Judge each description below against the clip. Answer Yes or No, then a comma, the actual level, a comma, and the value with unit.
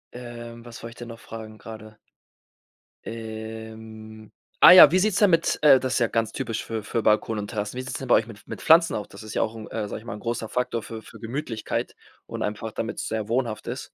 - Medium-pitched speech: No, low, 115 Hz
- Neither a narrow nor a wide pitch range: No, narrow, 1.8 semitones